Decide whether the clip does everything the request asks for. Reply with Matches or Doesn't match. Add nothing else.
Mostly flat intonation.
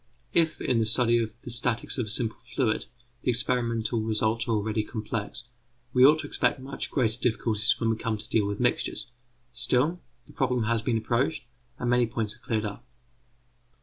Matches